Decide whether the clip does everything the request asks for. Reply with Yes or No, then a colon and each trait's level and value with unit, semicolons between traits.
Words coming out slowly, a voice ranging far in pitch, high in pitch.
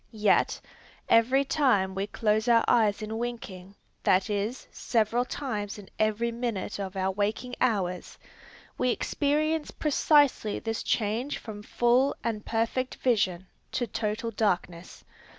No: slow, 130 wpm; average, 3.3 semitones; high, 225 Hz